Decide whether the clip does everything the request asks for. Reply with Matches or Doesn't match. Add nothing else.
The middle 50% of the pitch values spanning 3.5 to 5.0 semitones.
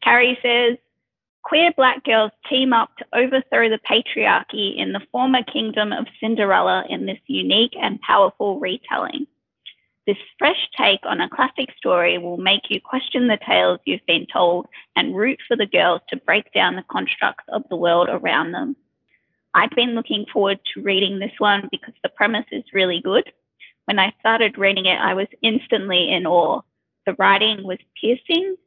Matches